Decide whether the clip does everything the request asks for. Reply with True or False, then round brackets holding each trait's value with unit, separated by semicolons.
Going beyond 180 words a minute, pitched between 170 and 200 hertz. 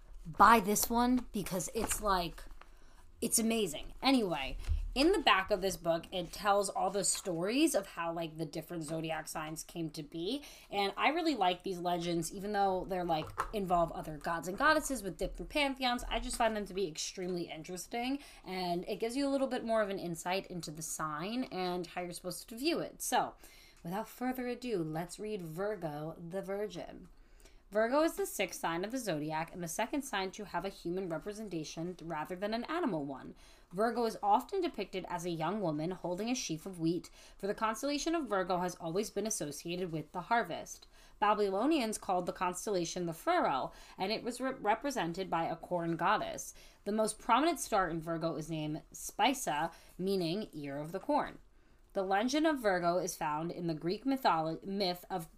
True (190 wpm; 190 Hz)